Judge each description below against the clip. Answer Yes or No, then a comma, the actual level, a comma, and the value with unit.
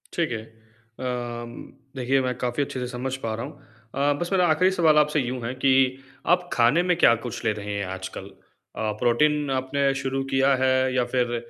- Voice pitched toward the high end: No, low, 130 Hz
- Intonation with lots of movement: No, average, 3.5 semitones